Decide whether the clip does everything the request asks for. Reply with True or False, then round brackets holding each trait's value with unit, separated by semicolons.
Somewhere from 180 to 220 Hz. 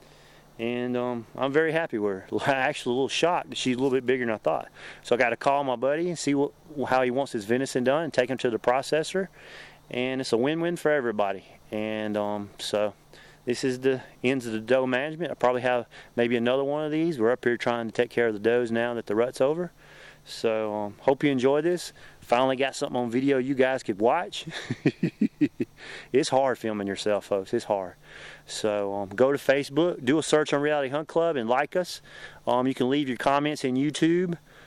False (130 Hz)